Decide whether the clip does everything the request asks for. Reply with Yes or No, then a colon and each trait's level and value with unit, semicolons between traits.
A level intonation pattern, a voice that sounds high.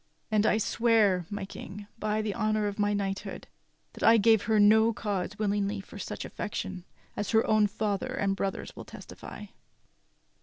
Yes: narrow, 1.5 semitones; high, 210 Hz